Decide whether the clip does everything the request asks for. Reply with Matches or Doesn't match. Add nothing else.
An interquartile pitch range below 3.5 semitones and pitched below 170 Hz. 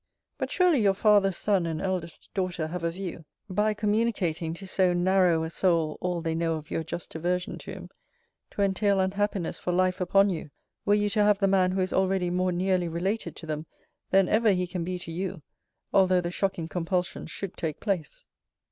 Doesn't match